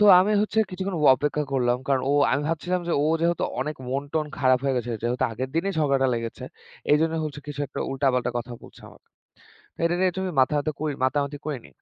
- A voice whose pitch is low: No, medium, 145 Hz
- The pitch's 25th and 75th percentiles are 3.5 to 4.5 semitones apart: Yes, average, 3.9 semitones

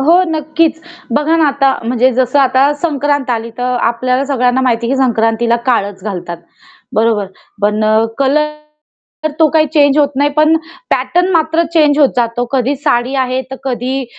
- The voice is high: Yes, very high, 265 Hz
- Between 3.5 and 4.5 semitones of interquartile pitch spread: Yes, average, 3.8 semitones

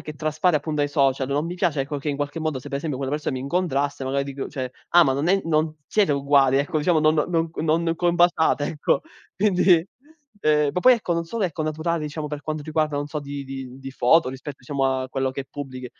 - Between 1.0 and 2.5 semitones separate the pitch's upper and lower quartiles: No, average, 2.9 semitones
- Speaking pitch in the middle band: Yes, medium, 150 Hz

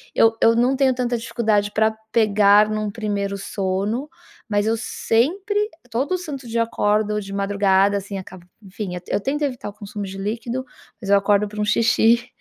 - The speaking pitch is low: No, high, 215 Hz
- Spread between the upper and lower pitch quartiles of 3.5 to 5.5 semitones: No, average, 2.8 semitones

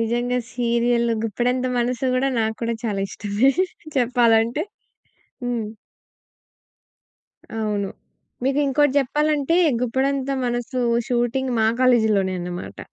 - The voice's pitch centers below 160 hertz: No, high, 240 Hz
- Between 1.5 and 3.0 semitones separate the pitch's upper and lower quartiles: Yes, narrow, 2.6 semitones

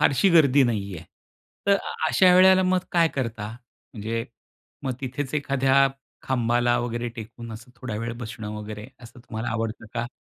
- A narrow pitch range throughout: No, average, 3.6 semitones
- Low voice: Yes, low, 120 Hz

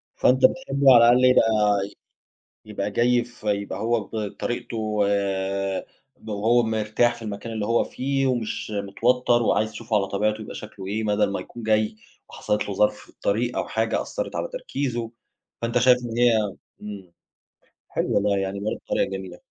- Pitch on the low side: Yes, low, 110 Hz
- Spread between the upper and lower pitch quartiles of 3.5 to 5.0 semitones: No, narrow, 2.5 semitones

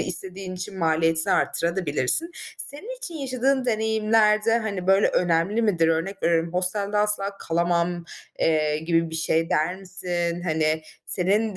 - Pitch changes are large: No, average, 4.2 semitones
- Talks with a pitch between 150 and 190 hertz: Yes, medium, 185 Hz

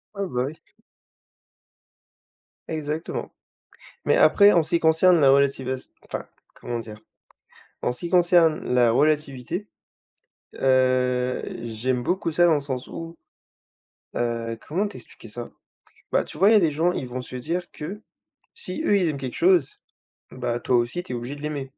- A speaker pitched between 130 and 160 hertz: Yes, medium, 140 Hz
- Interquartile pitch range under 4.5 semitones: No, average, 5.3 semitones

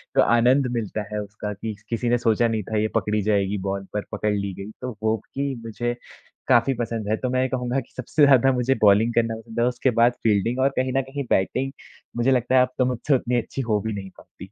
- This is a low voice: Yes, low, 115 Hz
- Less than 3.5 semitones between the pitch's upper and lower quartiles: Yes, average, 3.1 semitones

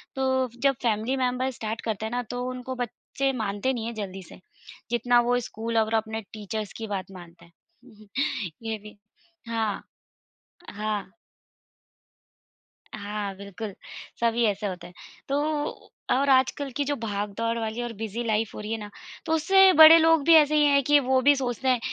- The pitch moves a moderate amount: Yes, average, 3.7 semitones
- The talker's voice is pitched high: Yes, high, 230 Hz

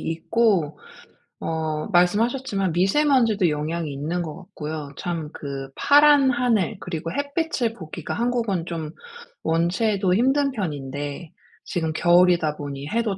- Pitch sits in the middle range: Yes, medium, 180 Hz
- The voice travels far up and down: Yes, wide, 6.6 semitones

